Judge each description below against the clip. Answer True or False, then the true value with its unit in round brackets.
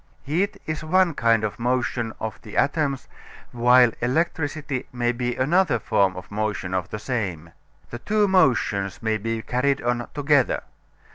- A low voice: True (125 Hz)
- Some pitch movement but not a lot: True (4.8 semitones)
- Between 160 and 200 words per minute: False (150 wpm)